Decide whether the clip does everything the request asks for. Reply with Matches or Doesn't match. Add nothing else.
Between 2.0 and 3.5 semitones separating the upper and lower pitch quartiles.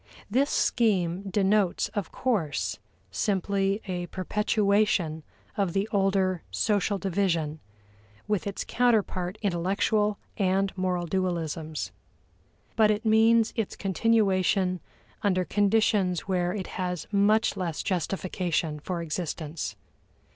Matches